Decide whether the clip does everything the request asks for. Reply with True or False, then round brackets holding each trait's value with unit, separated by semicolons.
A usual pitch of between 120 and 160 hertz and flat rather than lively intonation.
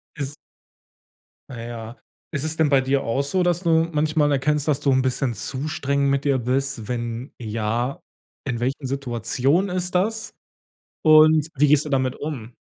False (140 Hz; 3.5 semitones)